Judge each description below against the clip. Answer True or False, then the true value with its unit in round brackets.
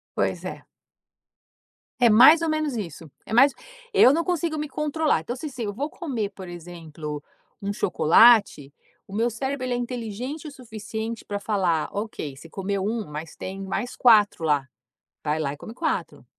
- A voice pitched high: True (220 Hz)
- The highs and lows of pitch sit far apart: True (6.8 semitones)